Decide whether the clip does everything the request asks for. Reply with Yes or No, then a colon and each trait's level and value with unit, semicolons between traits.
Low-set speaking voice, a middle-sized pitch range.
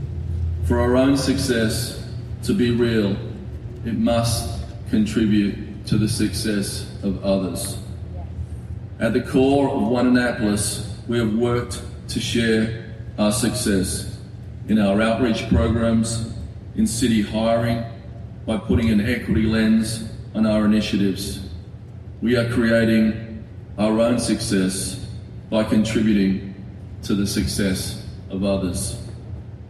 No: low, 110 Hz; narrow, 2.2 semitones